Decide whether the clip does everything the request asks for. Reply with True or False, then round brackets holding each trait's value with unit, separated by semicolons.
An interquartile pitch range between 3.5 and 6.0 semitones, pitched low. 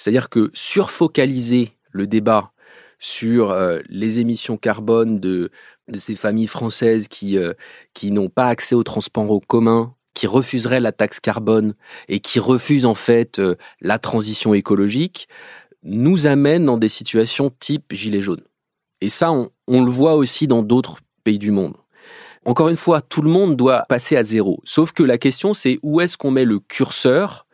True (4.0 semitones; 120 Hz)